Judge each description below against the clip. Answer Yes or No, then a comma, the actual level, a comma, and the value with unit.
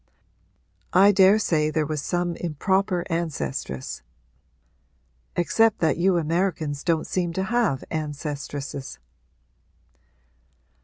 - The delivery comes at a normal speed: No, slow, 90 wpm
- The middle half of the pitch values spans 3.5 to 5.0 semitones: Yes, average, 3.9 semitones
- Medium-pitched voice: Yes, medium, 170 Hz